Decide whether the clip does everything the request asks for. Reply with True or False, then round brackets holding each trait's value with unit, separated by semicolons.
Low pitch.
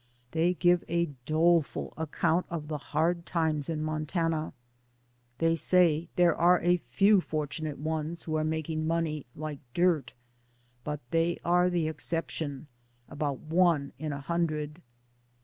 False (160 Hz)